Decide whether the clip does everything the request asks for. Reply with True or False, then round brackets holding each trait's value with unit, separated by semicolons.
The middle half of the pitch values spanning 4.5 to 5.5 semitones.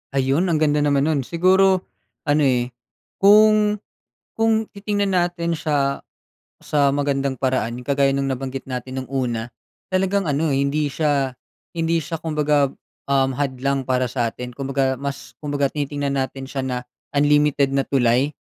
False (3.2 semitones)